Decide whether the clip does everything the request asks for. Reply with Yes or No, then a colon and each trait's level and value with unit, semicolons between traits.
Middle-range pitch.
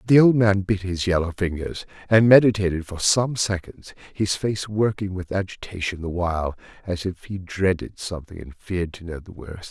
No: very low, 95 Hz